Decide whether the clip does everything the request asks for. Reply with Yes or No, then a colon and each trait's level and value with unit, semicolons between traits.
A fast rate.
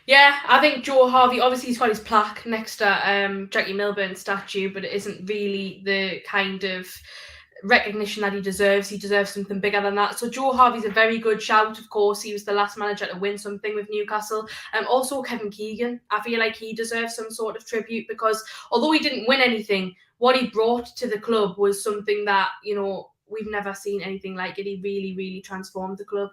Yes: fast, 215 wpm